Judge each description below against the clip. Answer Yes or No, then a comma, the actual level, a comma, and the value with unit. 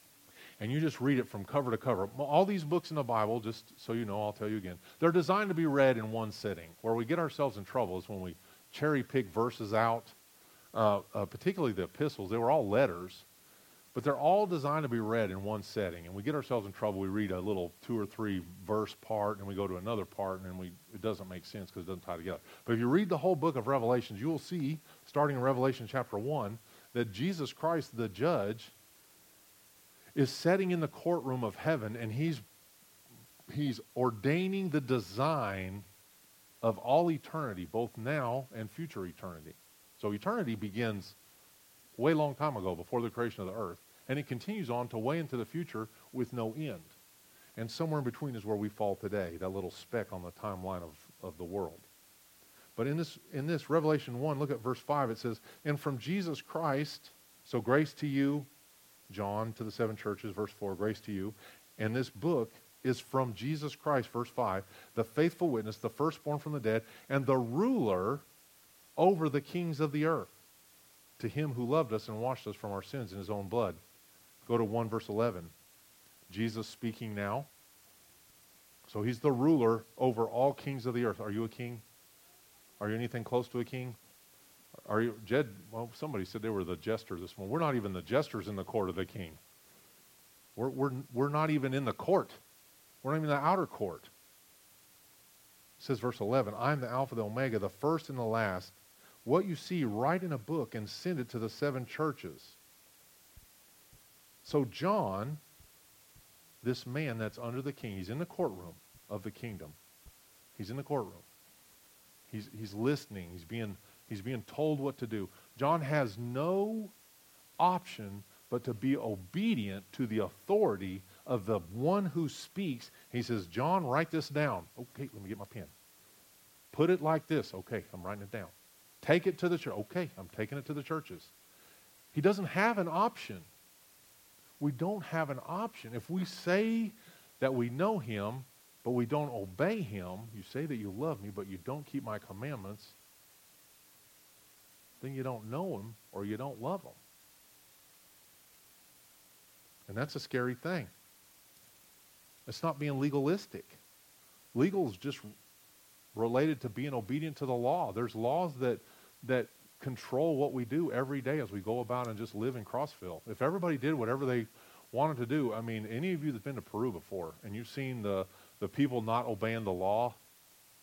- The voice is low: Yes, low, 120 Hz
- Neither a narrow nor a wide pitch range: No, wide, 5.9 semitones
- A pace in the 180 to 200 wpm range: Yes, average, 190 wpm